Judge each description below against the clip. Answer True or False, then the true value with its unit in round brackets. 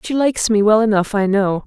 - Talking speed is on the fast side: True (250 wpm)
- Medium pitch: False (215 Hz)